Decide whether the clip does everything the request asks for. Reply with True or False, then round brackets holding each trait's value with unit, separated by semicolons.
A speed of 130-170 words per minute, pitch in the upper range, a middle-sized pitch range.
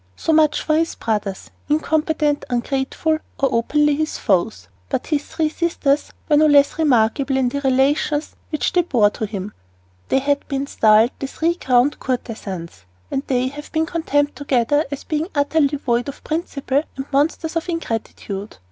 True (165 wpm; 280 Hz; 4.0 semitones)